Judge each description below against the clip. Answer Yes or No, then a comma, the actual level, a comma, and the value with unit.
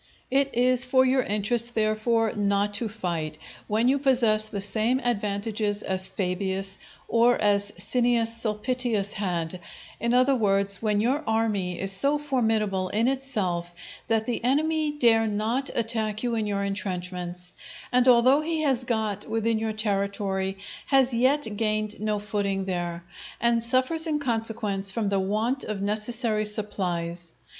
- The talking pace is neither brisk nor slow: Yes, average, 145 wpm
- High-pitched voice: Yes, high, 215 Hz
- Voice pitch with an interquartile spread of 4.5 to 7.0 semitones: No, average, 3.5 semitones